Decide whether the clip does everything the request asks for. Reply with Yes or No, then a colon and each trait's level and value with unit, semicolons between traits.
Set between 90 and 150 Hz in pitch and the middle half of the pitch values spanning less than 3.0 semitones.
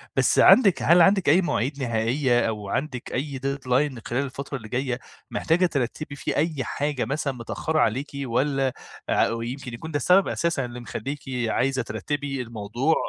No: low, 135 Hz; average, 3.5 semitones